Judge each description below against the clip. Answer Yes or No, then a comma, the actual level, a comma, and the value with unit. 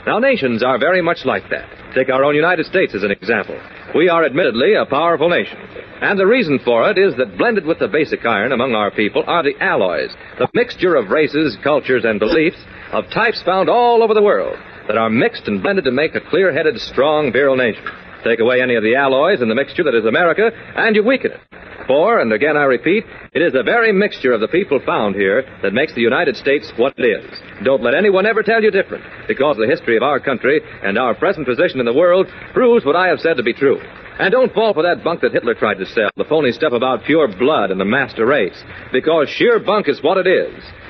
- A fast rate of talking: Yes, fast, 235 wpm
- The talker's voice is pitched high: Yes, high, 215 Hz